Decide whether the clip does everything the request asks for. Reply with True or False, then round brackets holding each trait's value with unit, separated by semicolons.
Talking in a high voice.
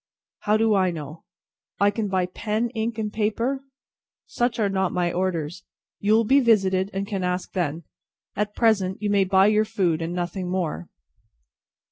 True (195 Hz)